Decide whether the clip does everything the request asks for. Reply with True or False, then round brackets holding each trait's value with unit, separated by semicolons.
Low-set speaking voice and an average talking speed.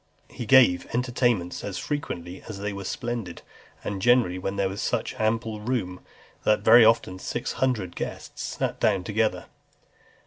True (105 Hz; 160 wpm)